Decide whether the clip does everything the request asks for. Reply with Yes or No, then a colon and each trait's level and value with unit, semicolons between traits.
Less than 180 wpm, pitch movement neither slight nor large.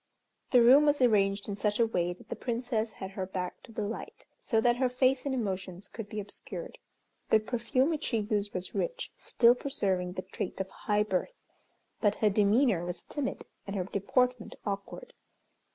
No: average, 185 wpm; average, 4.1 semitones